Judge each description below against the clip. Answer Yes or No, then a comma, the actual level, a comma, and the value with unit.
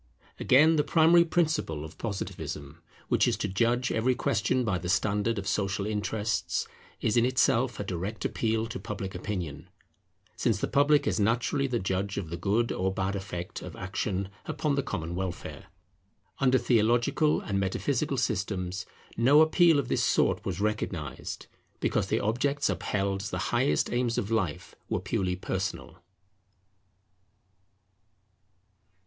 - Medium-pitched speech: No, low, 105 Hz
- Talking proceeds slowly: No, average, 145 wpm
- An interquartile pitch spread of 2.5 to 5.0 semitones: Yes, average, 4.7 semitones